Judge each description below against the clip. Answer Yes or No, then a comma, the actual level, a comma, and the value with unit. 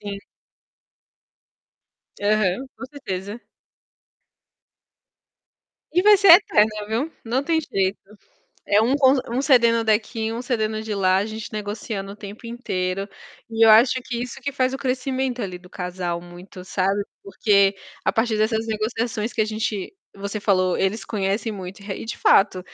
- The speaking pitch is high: Yes, high, 215 Hz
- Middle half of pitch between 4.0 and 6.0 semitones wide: No, average, 3.5 semitones